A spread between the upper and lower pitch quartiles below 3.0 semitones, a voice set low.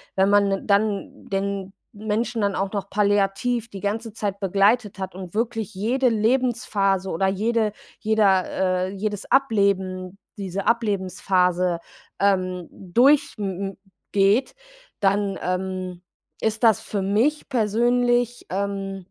No: narrow, 2.6 semitones; high, 200 Hz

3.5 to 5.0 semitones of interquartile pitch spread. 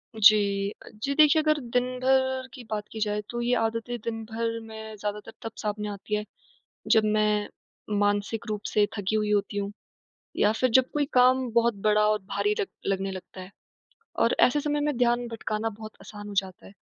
No: average, 2.8 semitones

